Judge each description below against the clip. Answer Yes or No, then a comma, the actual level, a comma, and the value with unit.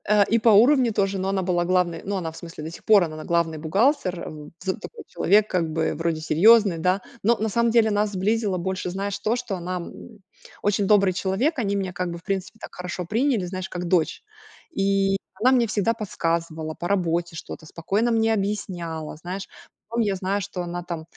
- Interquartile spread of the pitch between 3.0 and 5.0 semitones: Yes, average, 3.6 semitones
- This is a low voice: No, high, 190 Hz